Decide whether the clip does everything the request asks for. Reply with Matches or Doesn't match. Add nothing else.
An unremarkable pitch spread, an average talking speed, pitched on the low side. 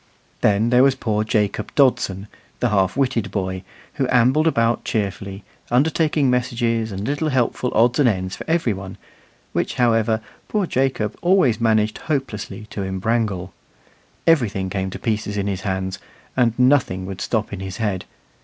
Matches